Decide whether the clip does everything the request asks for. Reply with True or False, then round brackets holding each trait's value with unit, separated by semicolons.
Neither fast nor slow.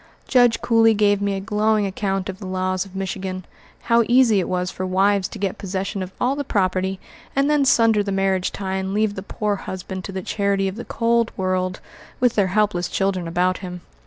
False (210 wpm)